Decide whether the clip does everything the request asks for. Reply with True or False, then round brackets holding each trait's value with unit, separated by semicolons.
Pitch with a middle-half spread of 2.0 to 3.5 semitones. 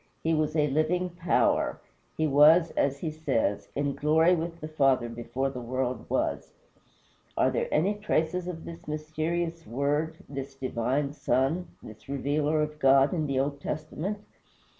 True (3.0 semitones)